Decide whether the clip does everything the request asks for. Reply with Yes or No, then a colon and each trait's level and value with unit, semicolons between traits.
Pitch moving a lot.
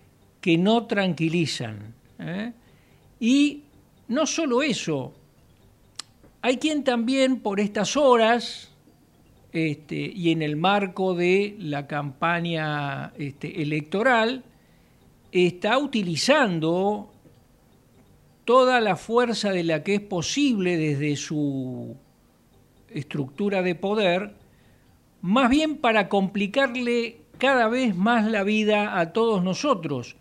Yes: wide, 6.9 semitones